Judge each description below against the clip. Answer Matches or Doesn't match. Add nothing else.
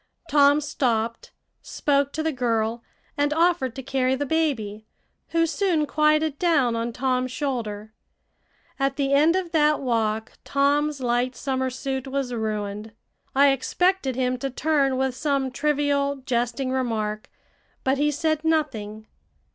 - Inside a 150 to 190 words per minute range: Doesn't match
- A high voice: Matches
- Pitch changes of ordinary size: Matches